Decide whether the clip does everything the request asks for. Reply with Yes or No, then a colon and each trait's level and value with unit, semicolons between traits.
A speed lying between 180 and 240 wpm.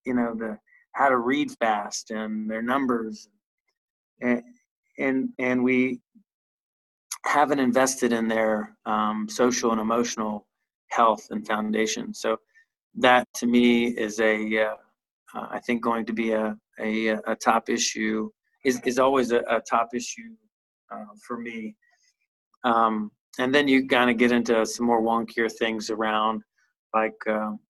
No: average, 145 wpm